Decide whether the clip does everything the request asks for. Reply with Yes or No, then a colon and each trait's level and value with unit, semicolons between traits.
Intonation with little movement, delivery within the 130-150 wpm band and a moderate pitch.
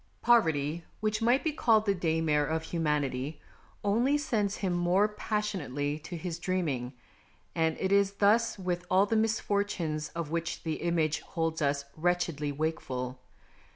No: average, 4.8 semitones; average, 145 wpm; medium, 170 Hz